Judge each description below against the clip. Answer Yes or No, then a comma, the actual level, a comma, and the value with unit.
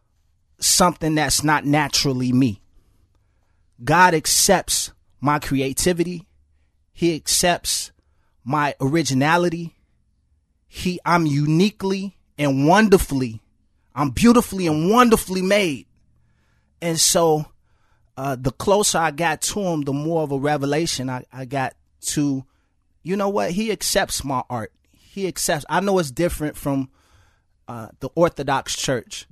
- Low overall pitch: No, medium, 145 Hz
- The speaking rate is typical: No, slow, 120 wpm